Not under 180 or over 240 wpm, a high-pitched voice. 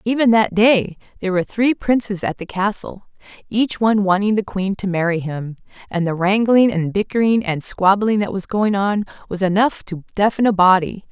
Yes: average, 190 wpm; high, 200 Hz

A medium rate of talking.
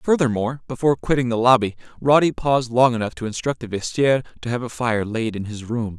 No: fast, 210 wpm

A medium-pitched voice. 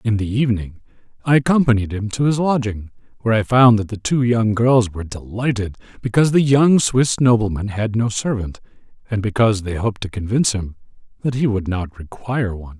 No: low, 110 Hz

